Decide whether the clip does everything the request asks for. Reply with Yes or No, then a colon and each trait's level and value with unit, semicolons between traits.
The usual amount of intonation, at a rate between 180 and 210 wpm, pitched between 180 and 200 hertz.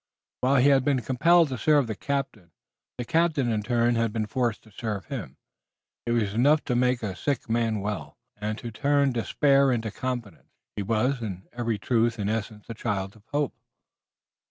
No: average, 3.8 semitones; average, 185 wpm; low, 115 Hz